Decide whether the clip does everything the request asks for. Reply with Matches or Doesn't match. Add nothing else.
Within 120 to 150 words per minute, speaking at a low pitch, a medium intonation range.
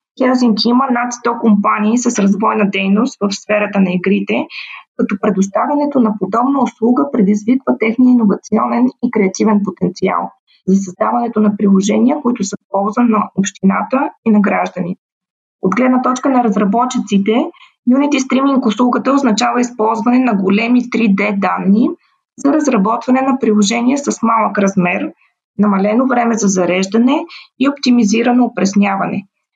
Doesn't match